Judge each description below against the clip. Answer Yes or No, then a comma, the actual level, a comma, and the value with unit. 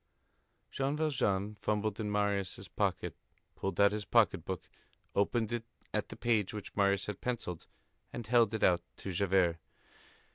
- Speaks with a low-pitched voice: Yes, low, 105 Hz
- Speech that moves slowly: No, average, 150 wpm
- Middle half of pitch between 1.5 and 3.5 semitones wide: Yes, narrow, 2.6 semitones